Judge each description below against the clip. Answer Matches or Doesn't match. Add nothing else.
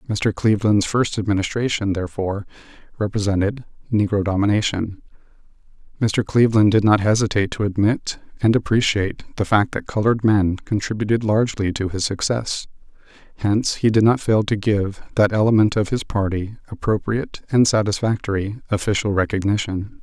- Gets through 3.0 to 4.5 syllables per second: Doesn't match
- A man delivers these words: Matches